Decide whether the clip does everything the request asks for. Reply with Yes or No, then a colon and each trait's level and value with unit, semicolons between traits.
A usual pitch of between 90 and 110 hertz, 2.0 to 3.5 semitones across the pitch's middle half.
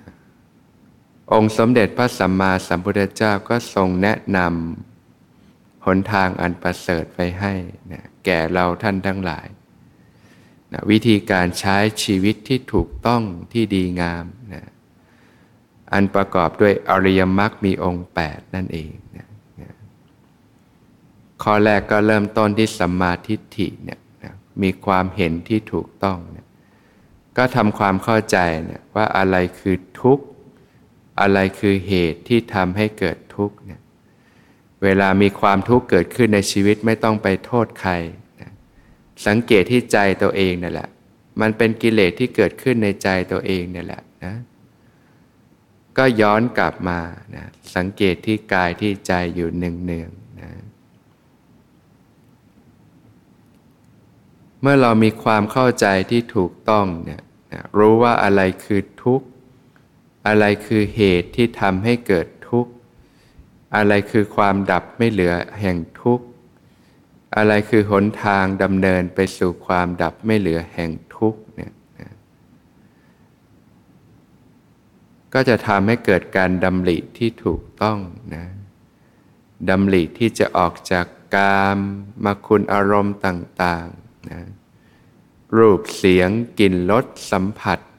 Yes: low, 100 Hz; average, 3.2 semitones